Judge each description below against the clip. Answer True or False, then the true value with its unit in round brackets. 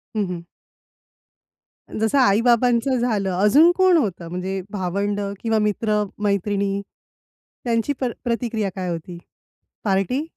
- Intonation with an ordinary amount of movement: True (3.5 semitones)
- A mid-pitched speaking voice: False (210 Hz)